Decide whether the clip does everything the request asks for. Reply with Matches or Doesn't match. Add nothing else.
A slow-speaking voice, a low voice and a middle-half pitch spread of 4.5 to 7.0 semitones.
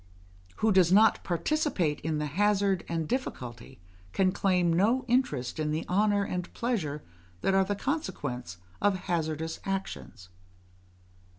Doesn't match